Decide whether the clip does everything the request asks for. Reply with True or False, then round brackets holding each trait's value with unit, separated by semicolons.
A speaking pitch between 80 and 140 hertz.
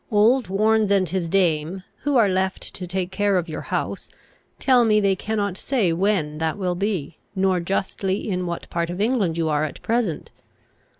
False (190 Hz)